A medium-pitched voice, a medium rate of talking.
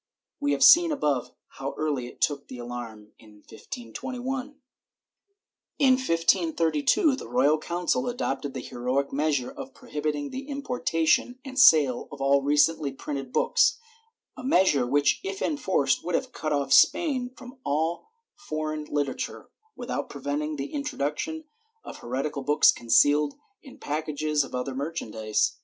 Yes: medium, 150 Hz; average, 145 wpm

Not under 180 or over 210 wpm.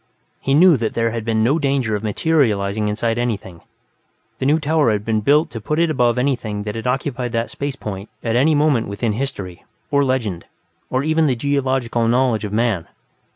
Yes: average, 195 wpm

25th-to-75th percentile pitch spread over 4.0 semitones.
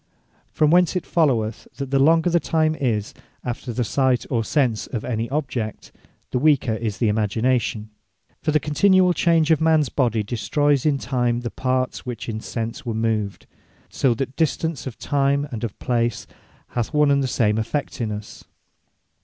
Yes: average, 4.7 semitones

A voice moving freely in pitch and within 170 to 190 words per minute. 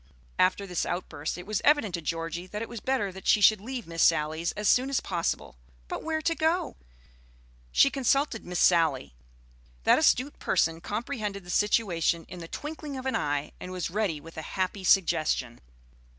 Yes: wide, 6.8 semitones; average, 180 wpm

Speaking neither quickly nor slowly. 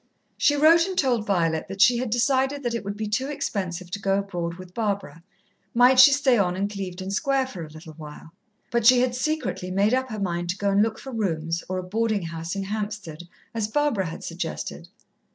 No: fast, 215 wpm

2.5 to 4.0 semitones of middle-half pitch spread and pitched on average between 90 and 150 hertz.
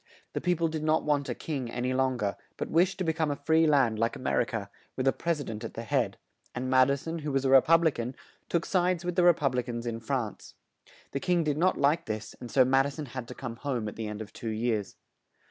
No: average, 5.2 semitones; low, 135 Hz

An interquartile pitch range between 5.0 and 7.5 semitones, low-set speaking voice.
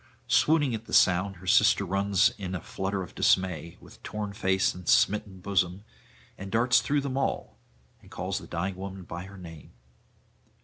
No: narrow, 2.4 semitones; very low, 95 Hz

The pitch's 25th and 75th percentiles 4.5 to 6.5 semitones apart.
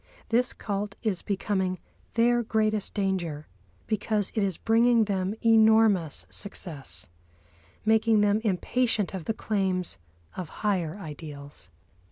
No: average, 3.2 semitones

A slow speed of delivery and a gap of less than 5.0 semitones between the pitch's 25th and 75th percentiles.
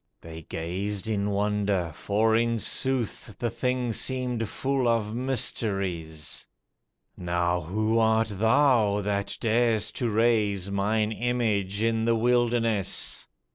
Yes: slow, 115 wpm; average, 2.8 semitones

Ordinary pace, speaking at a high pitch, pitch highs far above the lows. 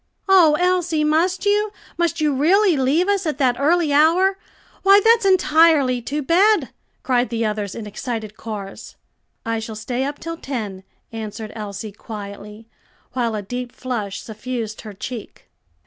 Yes: average, 150 wpm; very high, 260 Hz; wide, 7.3 semitones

